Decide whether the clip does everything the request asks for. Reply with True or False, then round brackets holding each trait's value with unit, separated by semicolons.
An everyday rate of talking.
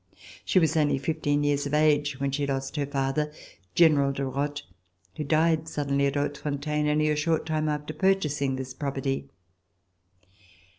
True (155 wpm)